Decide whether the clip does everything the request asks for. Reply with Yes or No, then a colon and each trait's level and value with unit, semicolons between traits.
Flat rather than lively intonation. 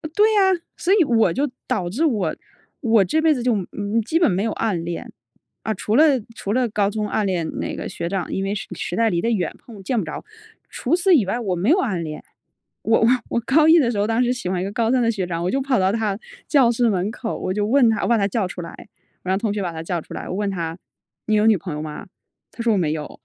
No: average, 4.6 semitones